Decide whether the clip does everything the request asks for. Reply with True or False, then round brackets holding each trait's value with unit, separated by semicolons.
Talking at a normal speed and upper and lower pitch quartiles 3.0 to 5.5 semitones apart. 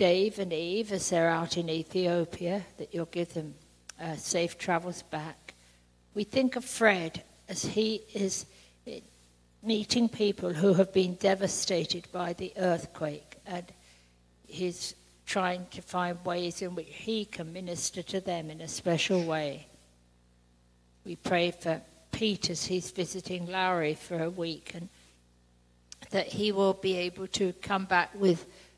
True (145 wpm; 3.4 semitones)